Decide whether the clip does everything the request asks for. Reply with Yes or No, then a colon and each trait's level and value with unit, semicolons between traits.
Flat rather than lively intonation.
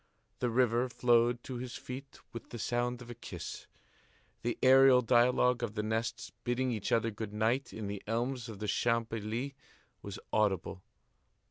Yes: narrow, 2.0 semitones